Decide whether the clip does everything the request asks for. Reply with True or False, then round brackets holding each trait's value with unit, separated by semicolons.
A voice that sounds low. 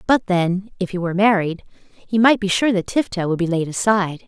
False (190 Hz)